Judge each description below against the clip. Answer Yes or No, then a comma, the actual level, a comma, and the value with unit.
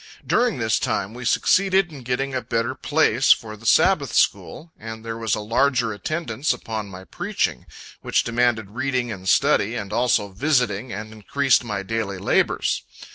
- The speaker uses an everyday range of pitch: Yes, average, 4.0 semitones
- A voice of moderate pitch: No, low, 115 Hz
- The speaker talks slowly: No, average, 165 wpm